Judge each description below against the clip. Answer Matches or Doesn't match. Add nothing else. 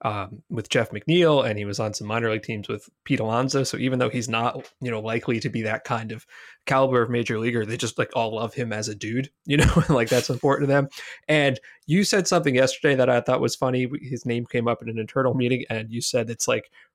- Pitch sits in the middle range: Doesn't match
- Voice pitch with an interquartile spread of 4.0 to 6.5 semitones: Doesn't match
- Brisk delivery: Matches